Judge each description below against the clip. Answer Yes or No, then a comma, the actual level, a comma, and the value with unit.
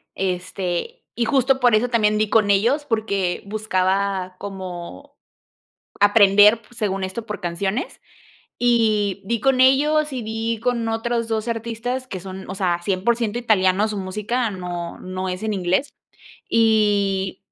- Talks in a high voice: Yes, high, 210 Hz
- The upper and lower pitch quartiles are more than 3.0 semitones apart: Yes, average, 3.6 semitones